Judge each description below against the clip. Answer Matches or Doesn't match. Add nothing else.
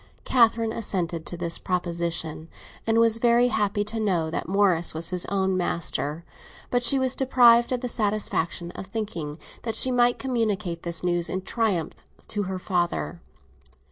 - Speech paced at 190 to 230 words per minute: Doesn't match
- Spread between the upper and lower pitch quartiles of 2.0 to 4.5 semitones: Doesn't match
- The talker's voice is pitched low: Doesn't match